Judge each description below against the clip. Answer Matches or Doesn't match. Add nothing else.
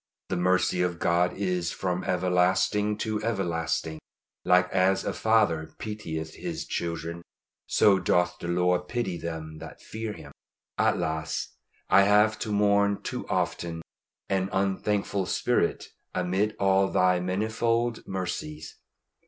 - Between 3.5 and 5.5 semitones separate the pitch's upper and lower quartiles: Doesn't match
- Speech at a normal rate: Doesn't match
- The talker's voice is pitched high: Doesn't match